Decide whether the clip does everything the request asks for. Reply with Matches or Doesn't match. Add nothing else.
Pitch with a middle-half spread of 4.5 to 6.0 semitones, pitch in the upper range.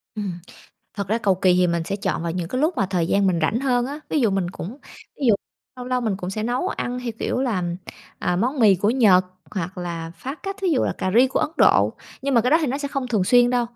Matches